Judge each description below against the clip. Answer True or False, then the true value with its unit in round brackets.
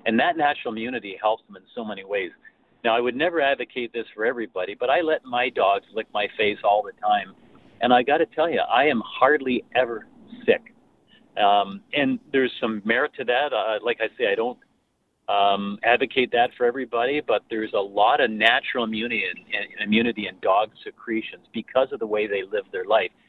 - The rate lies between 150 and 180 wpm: False (200 wpm)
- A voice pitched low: True (120 Hz)